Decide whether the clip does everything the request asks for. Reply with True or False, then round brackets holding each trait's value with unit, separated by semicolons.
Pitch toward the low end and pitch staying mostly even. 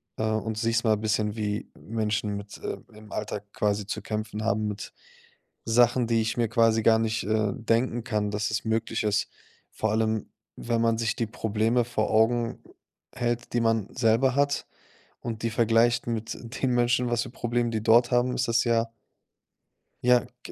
True (115 Hz; 1.6 semitones)